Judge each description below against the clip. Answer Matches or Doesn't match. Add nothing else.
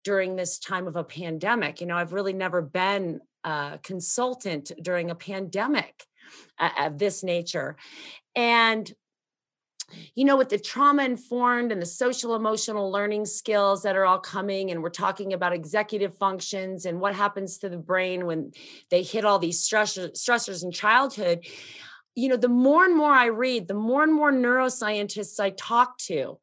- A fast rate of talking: Doesn't match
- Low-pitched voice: Doesn't match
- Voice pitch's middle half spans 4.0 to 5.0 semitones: Matches